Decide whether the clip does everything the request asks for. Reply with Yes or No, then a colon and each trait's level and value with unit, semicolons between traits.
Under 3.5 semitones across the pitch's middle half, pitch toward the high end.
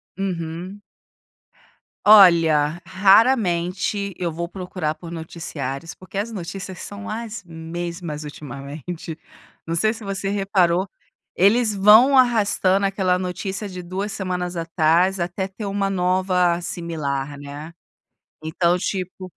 No: average, 2.9 semitones; medium, 180 Hz